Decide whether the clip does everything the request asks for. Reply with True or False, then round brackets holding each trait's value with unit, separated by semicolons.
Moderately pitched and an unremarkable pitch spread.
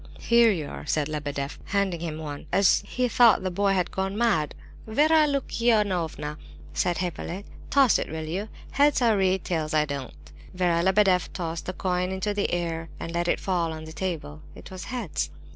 True (180 Hz; 4.3 semitones)